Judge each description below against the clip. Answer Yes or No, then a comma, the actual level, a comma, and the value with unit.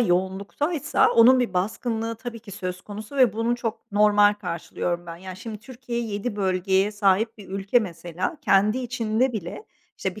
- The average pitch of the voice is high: Yes, high, 210 Hz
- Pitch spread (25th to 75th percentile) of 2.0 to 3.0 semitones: No, average, 3.6 semitones